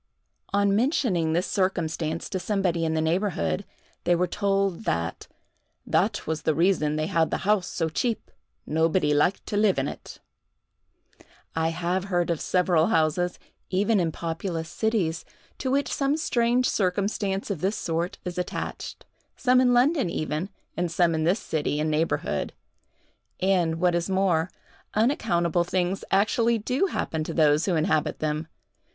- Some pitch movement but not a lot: Yes, average, 3.8 semitones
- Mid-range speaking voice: Yes, medium, 180 Hz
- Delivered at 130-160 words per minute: Yes, average, 150 wpm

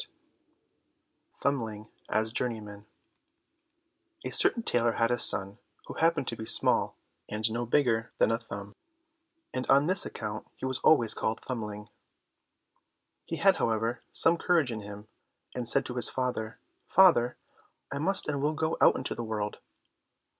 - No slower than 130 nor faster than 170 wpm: Yes, average, 155 wpm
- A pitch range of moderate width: Yes, average, 4.2 semitones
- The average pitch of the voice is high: No, low, 120 Hz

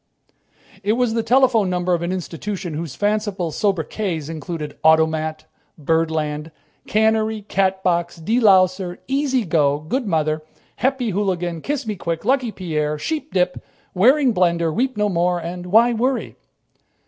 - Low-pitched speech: No, medium, 185 Hz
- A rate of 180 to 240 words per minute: No, slow, 135 wpm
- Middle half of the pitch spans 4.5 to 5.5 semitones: Yes, average, 5.1 semitones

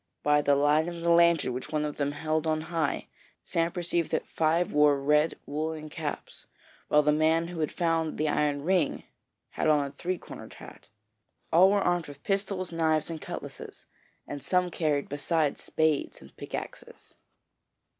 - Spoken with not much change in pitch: Yes, narrow, 2.3 semitones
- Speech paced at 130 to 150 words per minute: No, average, 170 wpm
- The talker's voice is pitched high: No, medium, 155 Hz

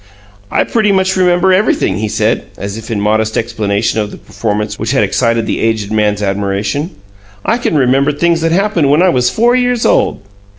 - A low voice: Yes, low, 125 Hz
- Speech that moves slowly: No, average, 195 wpm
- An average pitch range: No, wide, 8.8 semitones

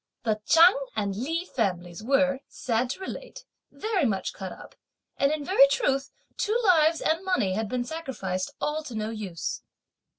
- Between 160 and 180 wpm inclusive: Yes, average, 165 wpm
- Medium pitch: No, very high, 270 Hz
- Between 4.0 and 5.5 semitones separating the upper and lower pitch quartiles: No, wide, 7.4 semitones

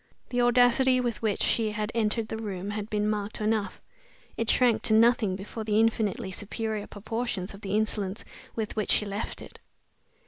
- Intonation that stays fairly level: Yes, narrow, 1.8 semitones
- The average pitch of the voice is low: No, high, 215 Hz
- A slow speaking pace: No, average, 175 wpm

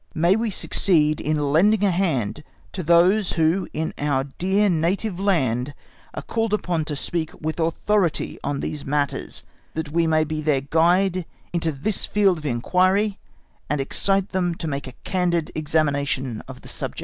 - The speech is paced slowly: No, average, 165 wpm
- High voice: No, medium, 165 Hz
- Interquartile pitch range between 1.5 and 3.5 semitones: No, average, 4.1 semitones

